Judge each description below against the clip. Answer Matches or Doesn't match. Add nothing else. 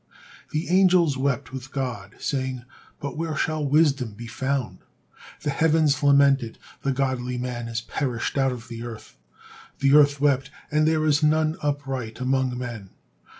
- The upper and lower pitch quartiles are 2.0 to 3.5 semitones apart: Matches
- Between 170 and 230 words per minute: Doesn't match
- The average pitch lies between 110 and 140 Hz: Matches